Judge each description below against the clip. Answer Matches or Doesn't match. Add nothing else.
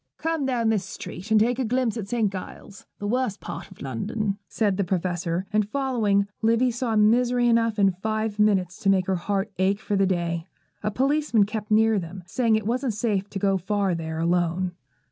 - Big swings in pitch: Doesn't match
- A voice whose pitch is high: Matches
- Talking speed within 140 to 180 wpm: Doesn't match